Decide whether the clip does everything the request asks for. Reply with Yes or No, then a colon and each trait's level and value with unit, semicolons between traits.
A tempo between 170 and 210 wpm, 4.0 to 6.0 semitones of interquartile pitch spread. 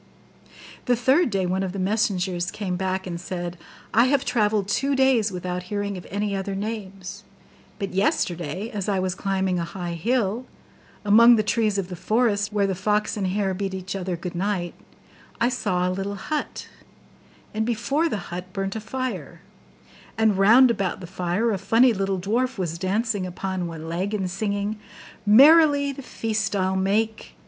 No: average, 175 wpm; average, 3.1 semitones